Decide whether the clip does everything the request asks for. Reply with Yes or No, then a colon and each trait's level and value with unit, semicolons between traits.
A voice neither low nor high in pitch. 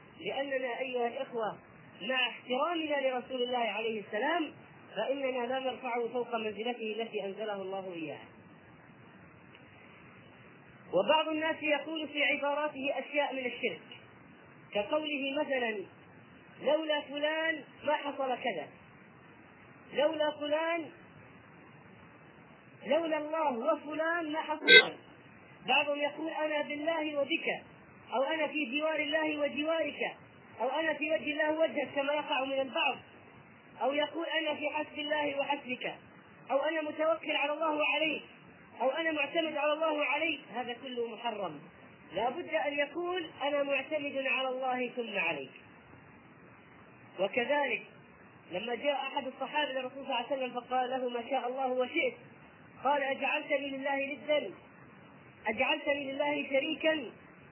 No: very high, 285 Hz